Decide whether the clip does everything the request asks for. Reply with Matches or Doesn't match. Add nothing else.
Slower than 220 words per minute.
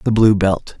Doesn't match